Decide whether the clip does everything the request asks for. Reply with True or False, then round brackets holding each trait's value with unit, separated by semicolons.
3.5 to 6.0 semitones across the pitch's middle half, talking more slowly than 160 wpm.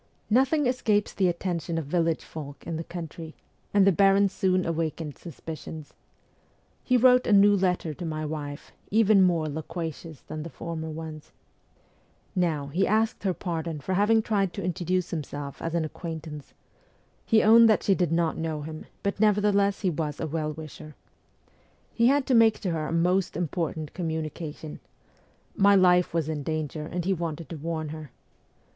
False (3.9 semitones; 170 wpm)